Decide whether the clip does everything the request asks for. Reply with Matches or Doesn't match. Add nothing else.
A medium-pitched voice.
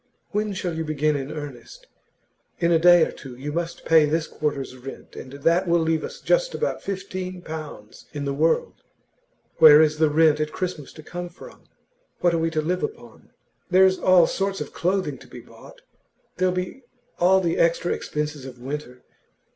Matches